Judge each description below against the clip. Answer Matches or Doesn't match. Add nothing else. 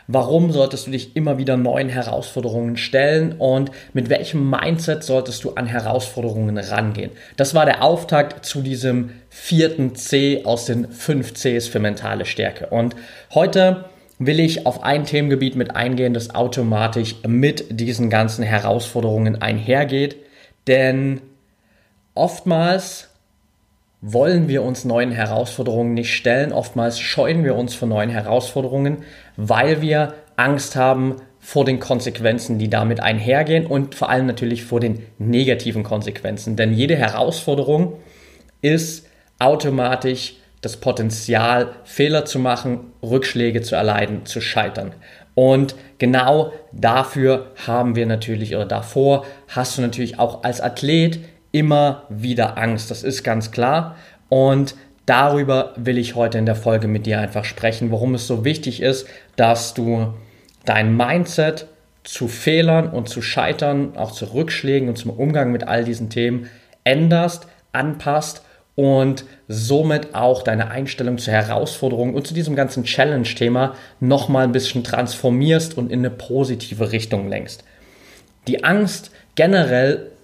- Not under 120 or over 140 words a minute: Matches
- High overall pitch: Doesn't match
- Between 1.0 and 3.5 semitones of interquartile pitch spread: Matches